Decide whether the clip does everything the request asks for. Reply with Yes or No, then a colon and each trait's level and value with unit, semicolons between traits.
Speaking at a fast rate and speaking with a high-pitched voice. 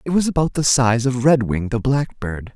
No: fast, 210 wpm; low, 130 Hz